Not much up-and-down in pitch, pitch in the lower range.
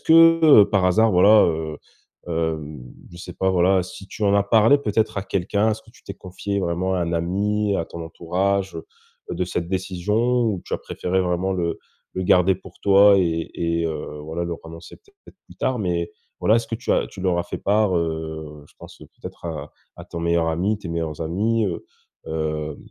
No: average, 3.4 semitones; very low, 90 Hz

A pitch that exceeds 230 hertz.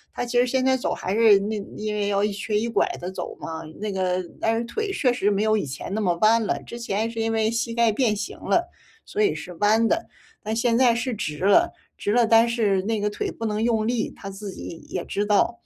No: high, 220 Hz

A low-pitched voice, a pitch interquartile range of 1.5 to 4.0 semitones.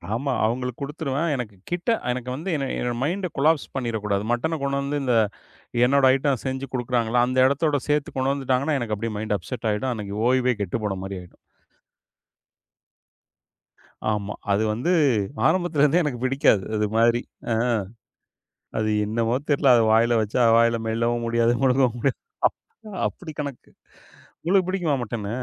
Yes: low, 125 Hz; average, 3.6 semitones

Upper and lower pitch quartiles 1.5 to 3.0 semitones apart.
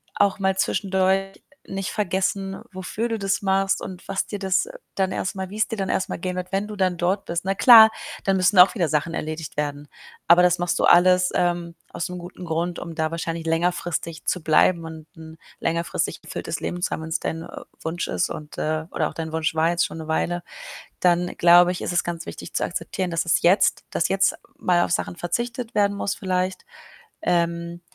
Yes: narrow, 2.4 semitones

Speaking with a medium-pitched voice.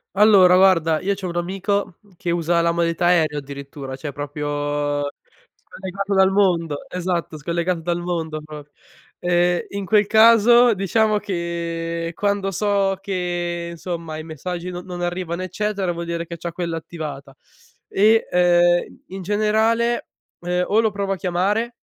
Yes: medium, 175 Hz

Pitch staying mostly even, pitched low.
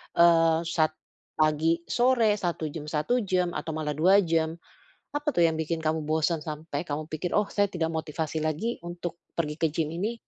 No: narrow, 2.1 semitones; medium, 165 Hz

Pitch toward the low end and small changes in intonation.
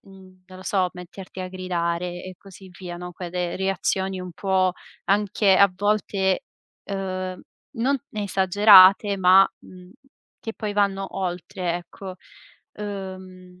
No: high, 190 Hz; narrow, 1.3 semitones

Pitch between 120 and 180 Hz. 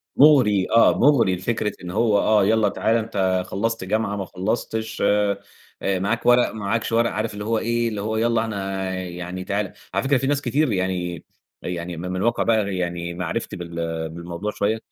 No: low, 105 Hz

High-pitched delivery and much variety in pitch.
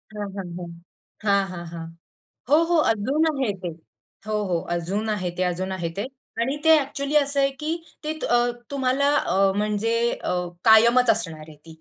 Yes: high, 215 Hz; wide, 6.8 semitones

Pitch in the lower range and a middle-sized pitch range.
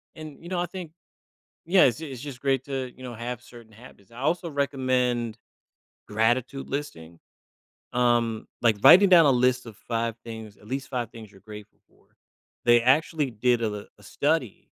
Yes: low, 125 Hz; average, 3.6 semitones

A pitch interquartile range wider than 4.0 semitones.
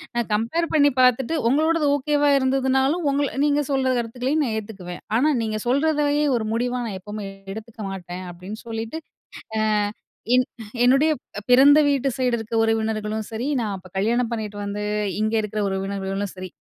Yes: average, 4.4 semitones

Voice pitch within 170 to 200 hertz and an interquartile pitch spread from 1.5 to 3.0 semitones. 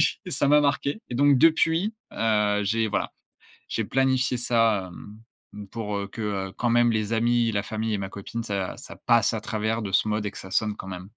No: low, 110 Hz; average, 2.7 semitones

